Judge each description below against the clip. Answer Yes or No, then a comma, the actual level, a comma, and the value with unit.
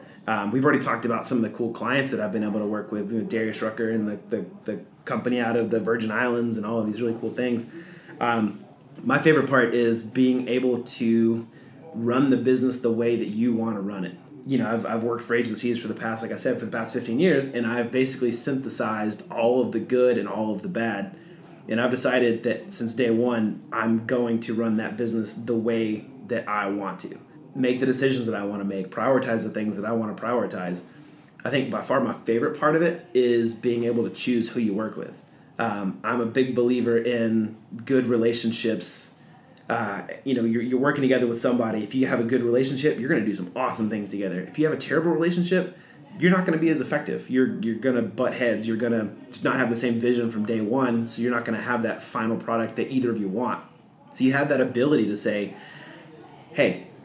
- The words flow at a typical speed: No, fast, 235 wpm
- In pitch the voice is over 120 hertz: No, low, 115 Hz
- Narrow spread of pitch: Yes, narrow, 2.1 semitones